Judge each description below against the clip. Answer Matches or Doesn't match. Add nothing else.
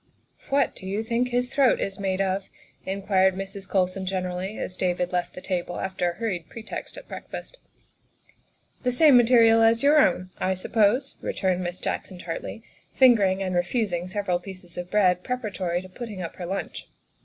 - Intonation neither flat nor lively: Matches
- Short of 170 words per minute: Doesn't match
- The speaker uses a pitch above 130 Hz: Matches